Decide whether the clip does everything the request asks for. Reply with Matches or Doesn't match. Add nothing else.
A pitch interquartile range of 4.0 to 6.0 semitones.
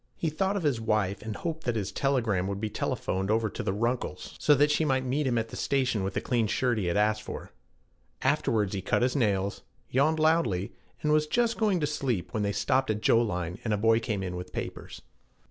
Matches